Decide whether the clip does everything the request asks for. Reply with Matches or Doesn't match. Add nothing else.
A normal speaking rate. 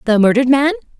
Matches